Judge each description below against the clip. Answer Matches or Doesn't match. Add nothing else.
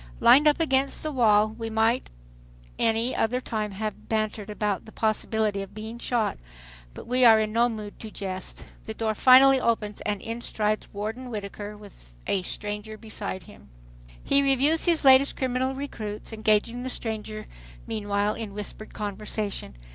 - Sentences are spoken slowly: Doesn't match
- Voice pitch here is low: Doesn't match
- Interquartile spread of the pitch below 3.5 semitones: Matches